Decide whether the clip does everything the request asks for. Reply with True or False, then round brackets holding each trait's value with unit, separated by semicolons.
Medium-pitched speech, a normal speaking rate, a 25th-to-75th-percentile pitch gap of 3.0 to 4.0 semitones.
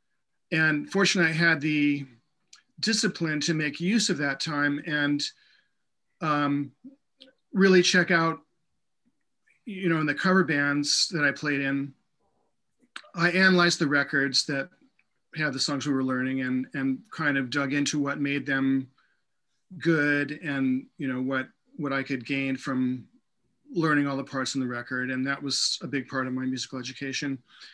True (145 Hz; 160 wpm; 3.6 semitones)